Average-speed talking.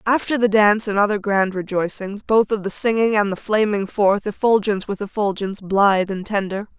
Yes: average, 185 wpm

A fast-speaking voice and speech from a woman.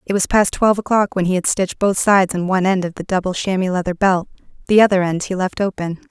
Yes: fast, 255 wpm; female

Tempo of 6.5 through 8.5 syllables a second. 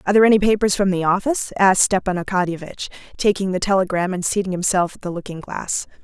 Yes: 6.7 syllables/s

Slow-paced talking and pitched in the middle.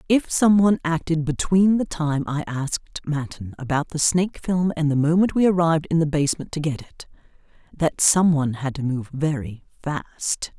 No: average, 185 wpm; medium, 155 Hz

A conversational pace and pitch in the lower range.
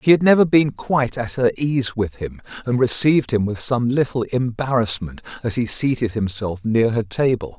Yes: average, 190 wpm; low, 120 Hz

